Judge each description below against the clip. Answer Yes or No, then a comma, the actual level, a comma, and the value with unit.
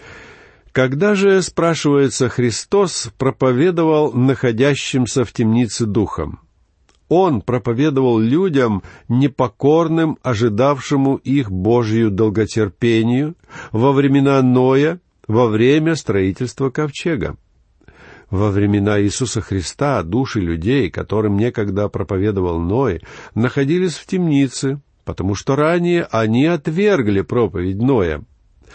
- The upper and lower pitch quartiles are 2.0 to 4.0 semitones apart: No, average, 4.9 semitones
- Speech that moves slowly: Yes, slow, 90 wpm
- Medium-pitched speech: No, low, 125 Hz